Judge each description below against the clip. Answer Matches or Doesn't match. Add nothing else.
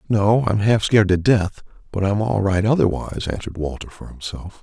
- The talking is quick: Doesn't match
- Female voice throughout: Doesn't match